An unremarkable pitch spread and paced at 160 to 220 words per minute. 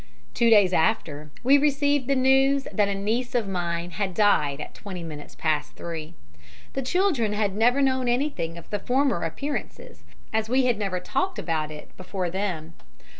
No: wide, 7.4 semitones; average, 175 wpm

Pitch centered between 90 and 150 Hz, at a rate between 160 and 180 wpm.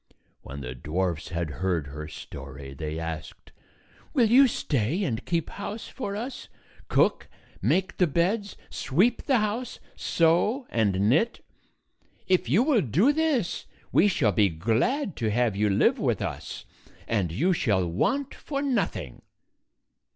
No: medium, 140 Hz; average, 145 wpm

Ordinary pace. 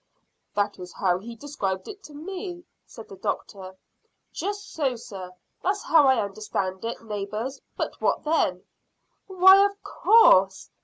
Yes: average, 145 wpm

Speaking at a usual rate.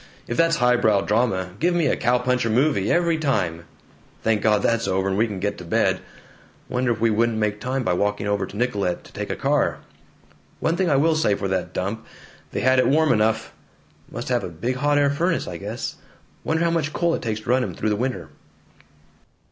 No: fast, 220 wpm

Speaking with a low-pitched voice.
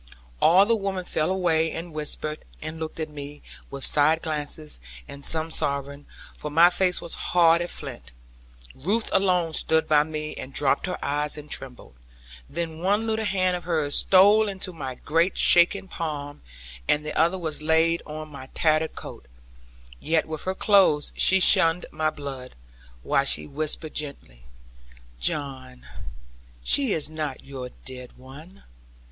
No: medium, 155 Hz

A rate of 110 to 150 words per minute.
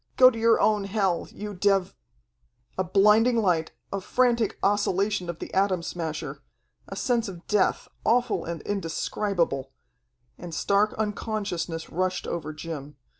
Yes: average, 140 wpm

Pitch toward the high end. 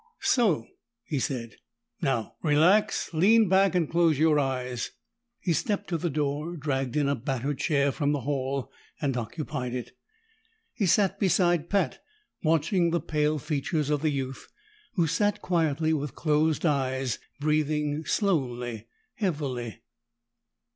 No: medium, 150 Hz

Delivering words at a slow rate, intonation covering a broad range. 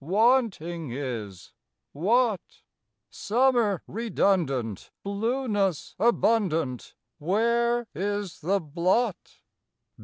Yes: slow, 65 wpm; wide, 6.4 semitones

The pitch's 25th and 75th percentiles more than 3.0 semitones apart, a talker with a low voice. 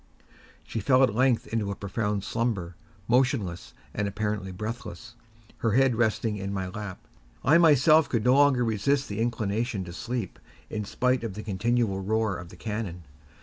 Yes: average, 3.6 semitones; low, 110 Hz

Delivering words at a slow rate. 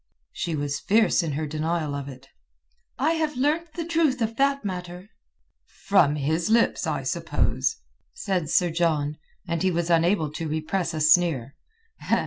No: average, 155 wpm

